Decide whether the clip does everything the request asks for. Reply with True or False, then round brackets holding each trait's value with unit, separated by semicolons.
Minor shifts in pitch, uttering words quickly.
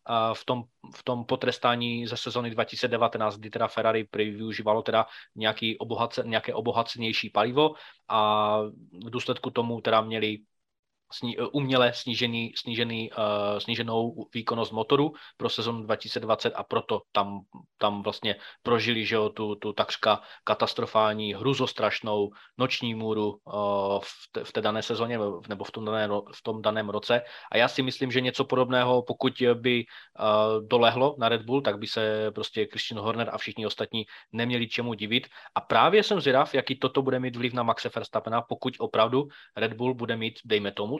False (2.2 semitones; 155 wpm)